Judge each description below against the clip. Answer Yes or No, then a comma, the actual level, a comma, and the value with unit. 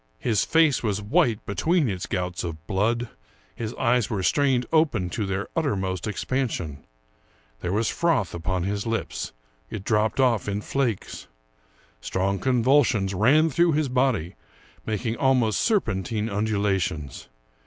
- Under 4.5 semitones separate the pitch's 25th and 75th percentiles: No, average, 5.2 semitones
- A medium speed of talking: No, slow, 130 wpm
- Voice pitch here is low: Yes, low, 110 Hz